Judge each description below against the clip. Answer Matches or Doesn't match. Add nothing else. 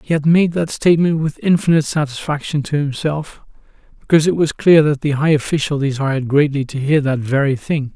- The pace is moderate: Matches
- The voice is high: Doesn't match